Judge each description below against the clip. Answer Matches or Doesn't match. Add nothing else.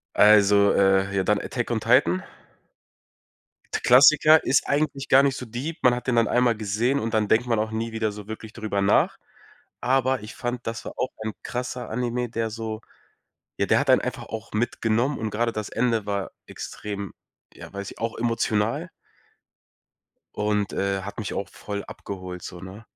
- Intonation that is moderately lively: Matches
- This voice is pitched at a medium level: Doesn't match